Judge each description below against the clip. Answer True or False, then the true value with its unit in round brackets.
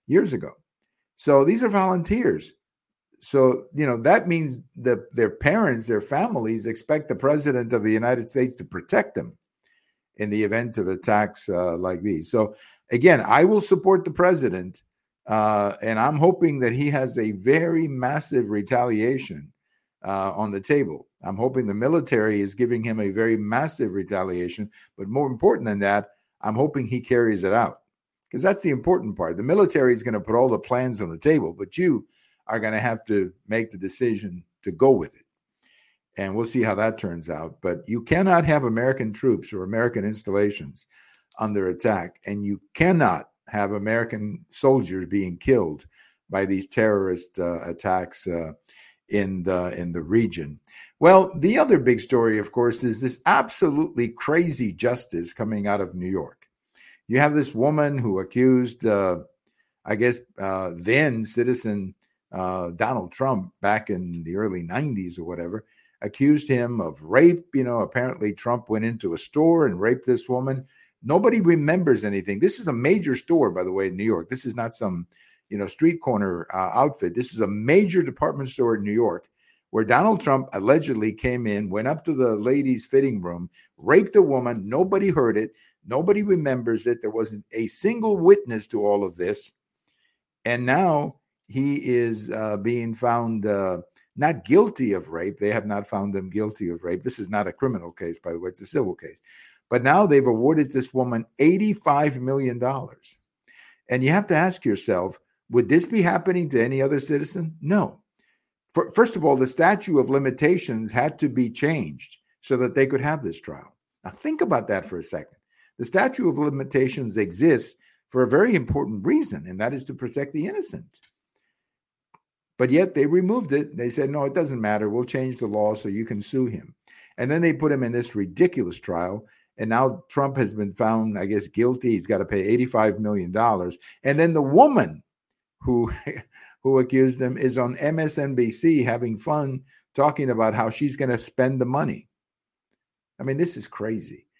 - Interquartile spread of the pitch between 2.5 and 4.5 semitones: False (5.4 semitones)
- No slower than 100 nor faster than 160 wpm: False (180 wpm)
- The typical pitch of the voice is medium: False (120 Hz)